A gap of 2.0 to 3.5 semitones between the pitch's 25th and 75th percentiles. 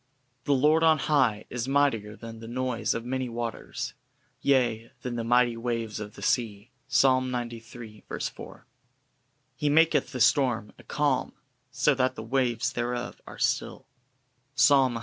Yes: average, 2.7 semitones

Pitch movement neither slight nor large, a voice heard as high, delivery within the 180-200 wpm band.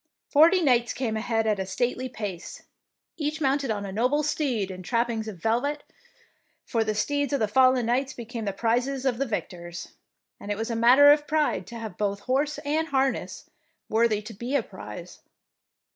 Yes: average, 4.2 semitones; high, 240 Hz; average, 190 wpm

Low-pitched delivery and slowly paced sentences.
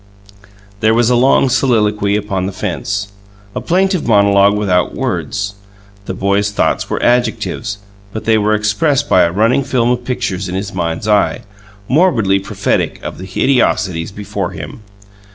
No: low, 105 Hz; average, 155 wpm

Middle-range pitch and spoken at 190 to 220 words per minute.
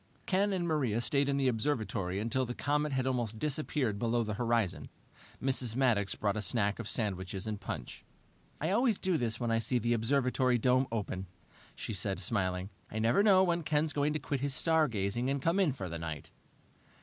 No: low, 120 Hz; average, 195 wpm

